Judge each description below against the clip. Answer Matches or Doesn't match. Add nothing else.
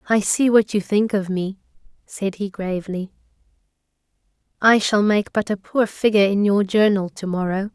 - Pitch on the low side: Doesn't match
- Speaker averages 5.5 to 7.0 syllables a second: Doesn't match